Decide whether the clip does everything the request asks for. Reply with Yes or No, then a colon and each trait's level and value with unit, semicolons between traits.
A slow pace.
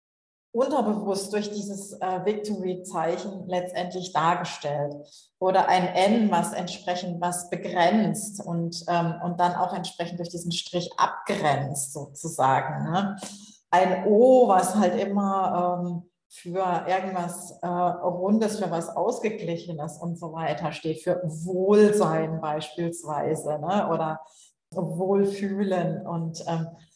Yes: slow, 115 wpm